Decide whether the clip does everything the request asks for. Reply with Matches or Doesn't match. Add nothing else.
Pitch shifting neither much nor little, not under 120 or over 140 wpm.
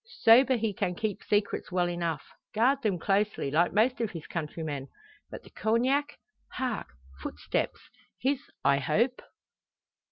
Doesn't match